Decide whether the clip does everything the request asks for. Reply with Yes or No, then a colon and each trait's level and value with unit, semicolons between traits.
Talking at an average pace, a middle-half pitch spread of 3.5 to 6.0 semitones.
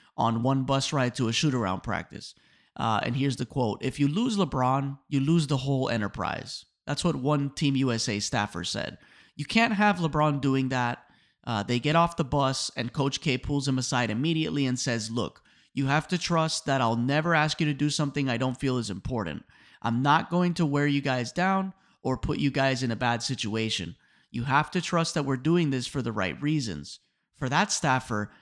No: fast, 210 wpm; average, 3.8 semitones